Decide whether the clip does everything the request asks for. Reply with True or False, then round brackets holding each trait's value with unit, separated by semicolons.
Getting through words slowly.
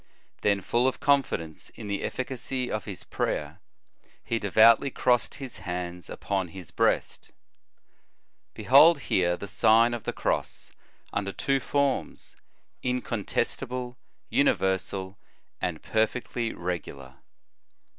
True (110 wpm)